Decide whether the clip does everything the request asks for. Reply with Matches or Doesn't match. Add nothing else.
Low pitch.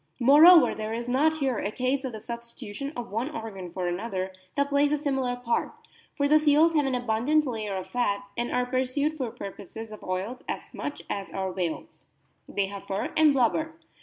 Doesn't match